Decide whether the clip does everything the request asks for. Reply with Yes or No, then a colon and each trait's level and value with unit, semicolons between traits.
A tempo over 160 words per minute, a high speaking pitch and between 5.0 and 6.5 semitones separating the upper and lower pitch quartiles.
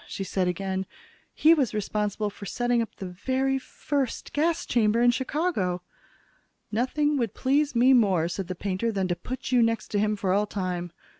Yes: average, 180 wpm; high, 215 Hz; average, 5.3 semitones